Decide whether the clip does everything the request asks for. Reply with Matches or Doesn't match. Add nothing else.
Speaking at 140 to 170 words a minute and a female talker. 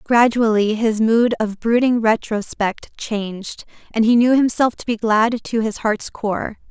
Matches